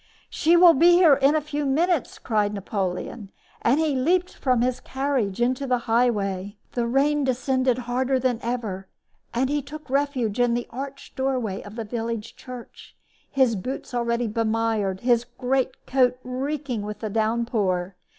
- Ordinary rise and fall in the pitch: Yes, average, 3.4 semitones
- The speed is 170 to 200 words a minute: No, average, 160 wpm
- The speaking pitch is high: Yes, very high, 250 Hz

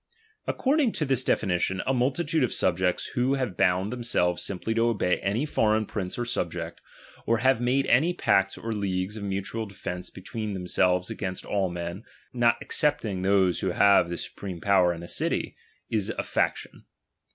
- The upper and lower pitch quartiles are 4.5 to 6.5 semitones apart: Yes, average, 4.8 semitones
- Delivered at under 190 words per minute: Yes, average, 170 wpm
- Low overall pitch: Yes, low, 100 Hz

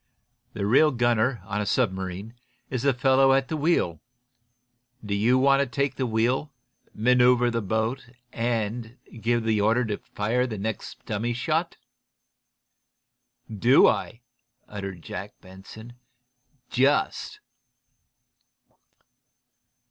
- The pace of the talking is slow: Yes, slow, 110 wpm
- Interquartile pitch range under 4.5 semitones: Yes, average, 3.6 semitones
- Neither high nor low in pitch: No, low, 120 Hz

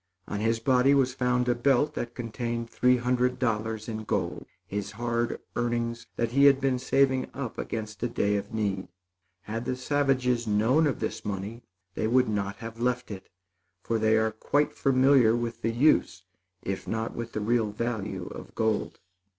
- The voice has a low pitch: Yes, low, 115 Hz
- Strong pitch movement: No, narrow, 2.5 semitones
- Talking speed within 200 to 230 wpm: No, average, 175 wpm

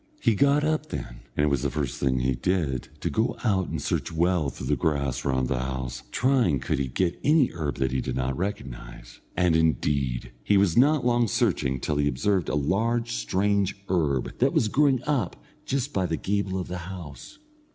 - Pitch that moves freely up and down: Yes, wide, 8.2 semitones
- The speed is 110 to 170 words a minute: No, fast, 205 wpm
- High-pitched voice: No, very low, 85 Hz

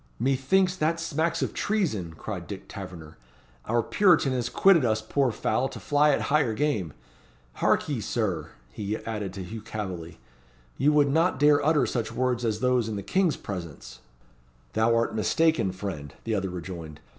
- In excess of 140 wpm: Yes, average, 170 wpm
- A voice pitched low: Yes, low, 115 Hz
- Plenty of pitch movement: Yes, wide, 7.2 semitones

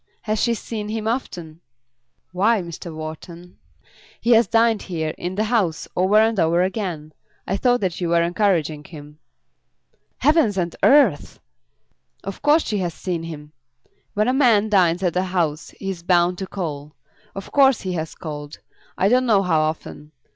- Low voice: No, medium, 185 Hz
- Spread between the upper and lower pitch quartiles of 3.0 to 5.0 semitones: Yes, average, 4.7 semitones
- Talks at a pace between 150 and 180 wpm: Yes, average, 170 wpm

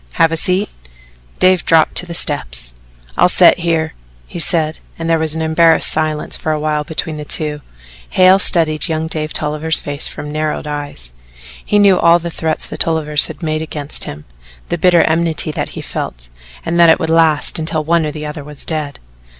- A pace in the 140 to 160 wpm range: No, average, 190 wpm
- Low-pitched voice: No, medium, 160 Hz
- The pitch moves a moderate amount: No, narrow, 1.7 semitones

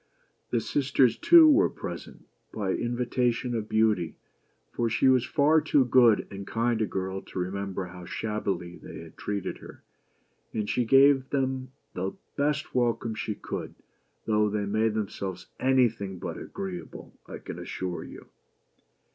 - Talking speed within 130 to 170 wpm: Yes, average, 150 wpm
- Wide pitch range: No, average, 4.6 semitones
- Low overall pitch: Yes, low, 110 Hz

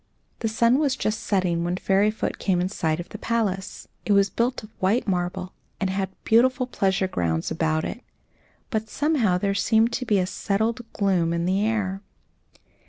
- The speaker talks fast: No, average, 175 wpm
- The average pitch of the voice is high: Yes, high, 200 Hz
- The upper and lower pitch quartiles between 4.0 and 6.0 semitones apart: No, average, 3.5 semitones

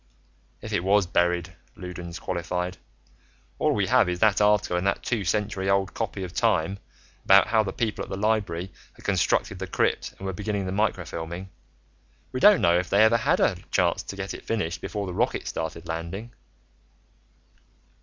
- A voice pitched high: No, very low, 95 Hz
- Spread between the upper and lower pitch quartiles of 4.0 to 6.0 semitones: No, average, 2.9 semitones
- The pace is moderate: Yes, average, 180 wpm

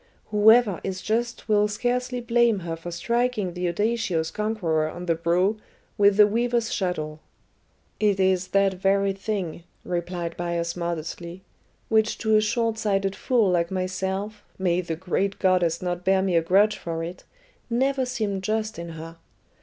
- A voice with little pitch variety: No, average, 3.8 semitones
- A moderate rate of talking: Yes, average, 155 wpm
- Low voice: No, high, 190 Hz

